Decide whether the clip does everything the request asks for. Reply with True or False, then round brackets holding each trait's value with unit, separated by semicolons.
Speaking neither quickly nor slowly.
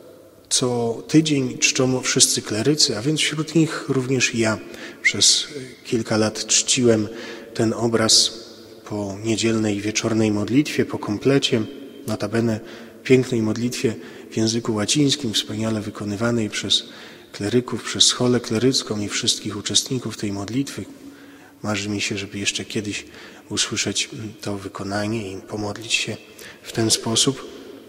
True (125 wpm)